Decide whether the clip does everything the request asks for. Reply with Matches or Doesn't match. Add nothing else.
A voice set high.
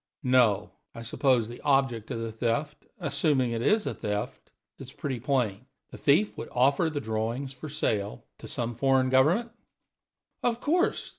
Doesn't match